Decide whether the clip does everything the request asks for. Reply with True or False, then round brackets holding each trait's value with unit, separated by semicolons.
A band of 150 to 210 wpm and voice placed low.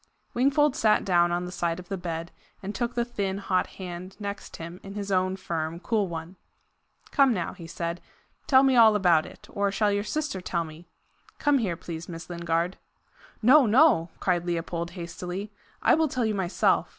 False (185 wpm; 185 Hz)